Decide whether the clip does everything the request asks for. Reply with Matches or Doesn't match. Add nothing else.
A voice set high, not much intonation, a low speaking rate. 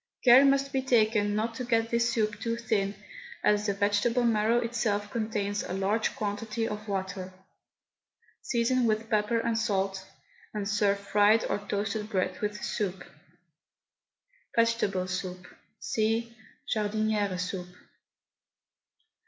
Matches